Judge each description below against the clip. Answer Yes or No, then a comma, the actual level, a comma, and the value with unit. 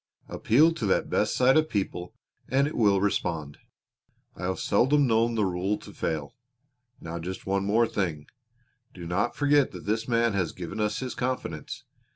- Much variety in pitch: Yes, wide, 5.8 semitones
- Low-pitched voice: Yes, low, 105 Hz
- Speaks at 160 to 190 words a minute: Yes, average, 175 wpm